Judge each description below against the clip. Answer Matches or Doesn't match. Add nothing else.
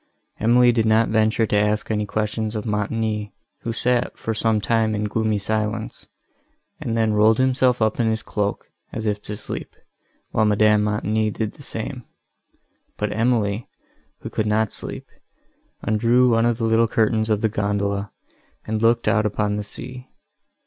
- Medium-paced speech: Matches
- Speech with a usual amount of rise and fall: Doesn't match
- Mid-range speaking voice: Doesn't match